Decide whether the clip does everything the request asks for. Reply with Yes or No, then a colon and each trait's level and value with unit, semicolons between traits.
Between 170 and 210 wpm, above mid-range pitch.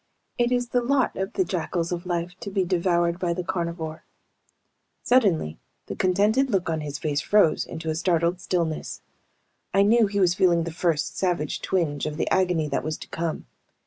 No: average, 185 wpm; medium, 175 Hz